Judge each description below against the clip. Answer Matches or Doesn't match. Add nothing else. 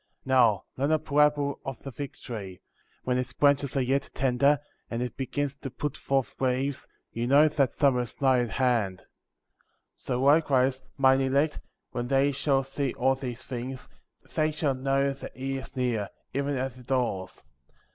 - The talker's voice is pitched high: Doesn't match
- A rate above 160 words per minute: Matches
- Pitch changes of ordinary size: Doesn't match